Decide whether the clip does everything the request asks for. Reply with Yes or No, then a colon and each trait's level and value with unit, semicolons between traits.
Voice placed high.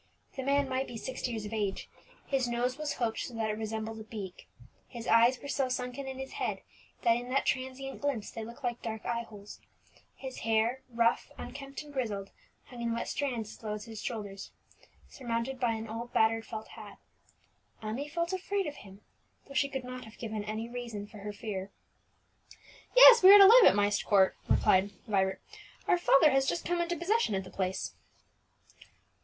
Yes: high, 235 Hz